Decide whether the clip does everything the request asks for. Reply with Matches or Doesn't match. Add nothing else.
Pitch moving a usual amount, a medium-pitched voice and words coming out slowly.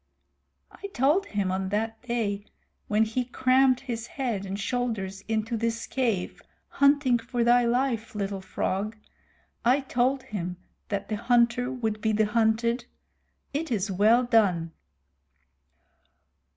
Doesn't match